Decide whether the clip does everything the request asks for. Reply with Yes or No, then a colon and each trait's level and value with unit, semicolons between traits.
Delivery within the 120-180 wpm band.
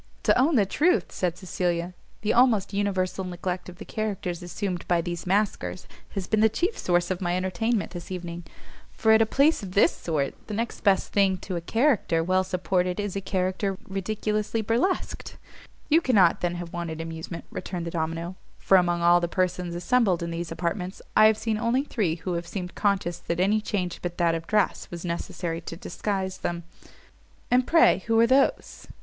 No: average, 190 wpm